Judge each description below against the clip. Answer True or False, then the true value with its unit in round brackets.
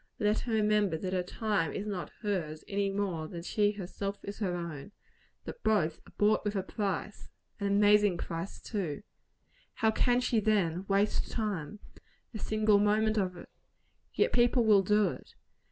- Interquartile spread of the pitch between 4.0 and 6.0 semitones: False (2.7 semitones)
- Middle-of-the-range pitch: False (205 Hz)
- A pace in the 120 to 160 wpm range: False (170 wpm)